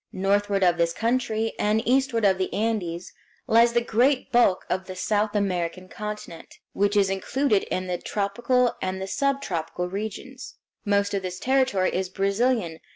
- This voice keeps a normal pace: Yes, average, 155 wpm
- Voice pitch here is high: Yes, high, 205 Hz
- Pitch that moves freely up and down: No, average, 4.0 semitones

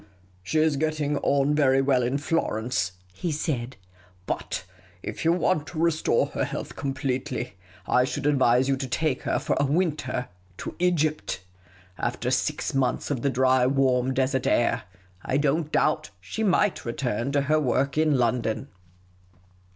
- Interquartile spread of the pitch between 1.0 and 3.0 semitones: No, average, 3.5 semitones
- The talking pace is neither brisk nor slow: Yes, average, 160 wpm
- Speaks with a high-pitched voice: No, low, 135 Hz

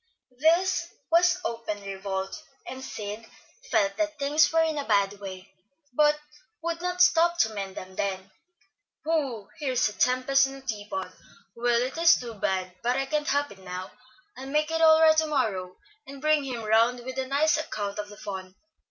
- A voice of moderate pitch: No, very high, 255 Hz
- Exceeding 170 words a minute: Yes, average, 185 wpm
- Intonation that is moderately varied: No, wide, 7.1 semitones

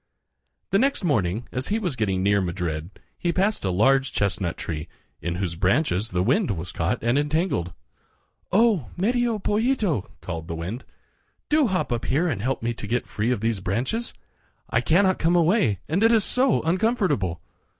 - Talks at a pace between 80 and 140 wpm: No, average, 175 wpm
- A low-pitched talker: Yes, low, 130 Hz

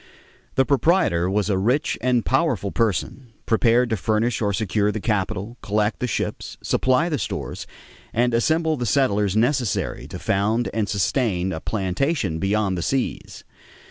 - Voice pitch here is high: No, low, 110 Hz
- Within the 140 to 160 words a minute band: Yes, average, 150 wpm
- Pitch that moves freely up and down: No, average, 4.1 semitones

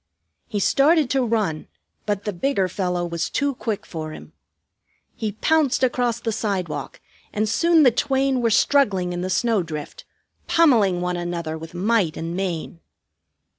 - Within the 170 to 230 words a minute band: No, average, 150 wpm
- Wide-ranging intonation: Yes, wide, 6.1 semitones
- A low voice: No, high, 205 Hz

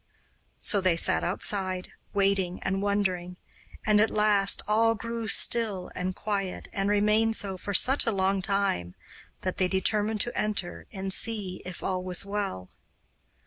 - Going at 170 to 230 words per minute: No, average, 150 wpm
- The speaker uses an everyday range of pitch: No, narrow, 2.3 semitones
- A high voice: Yes, high, 195 Hz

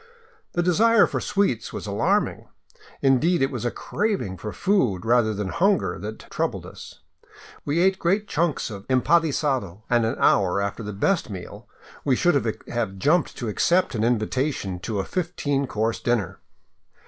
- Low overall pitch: Yes, low, 125 Hz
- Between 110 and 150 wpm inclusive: No, average, 160 wpm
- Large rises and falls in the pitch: Yes, wide, 8.4 semitones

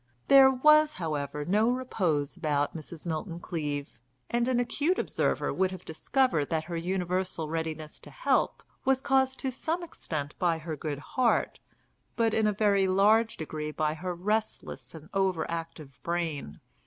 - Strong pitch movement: Yes, wide, 6.7 semitones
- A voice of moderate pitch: Yes, medium, 175 Hz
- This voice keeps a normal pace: Yes, average, 155 wpm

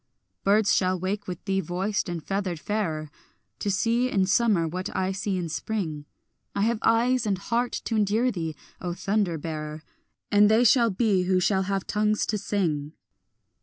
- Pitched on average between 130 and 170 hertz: No, high, 195 Hz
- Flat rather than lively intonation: No, average, 3.2 semitones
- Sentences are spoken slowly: No, average, 170 wpm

